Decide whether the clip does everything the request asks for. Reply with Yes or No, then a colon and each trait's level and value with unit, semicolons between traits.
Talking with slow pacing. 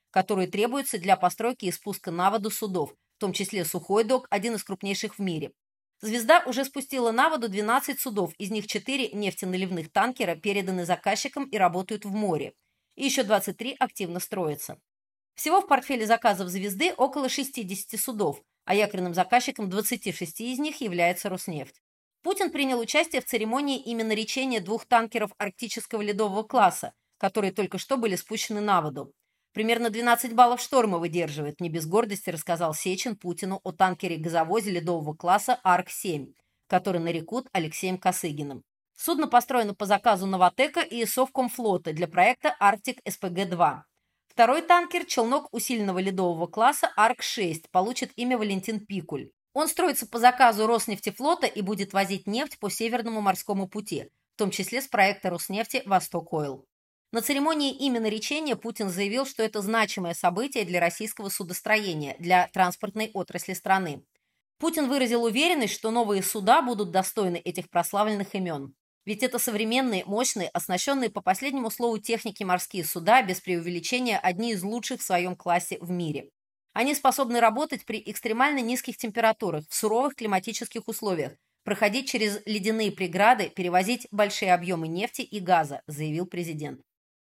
No: average, 145 wpm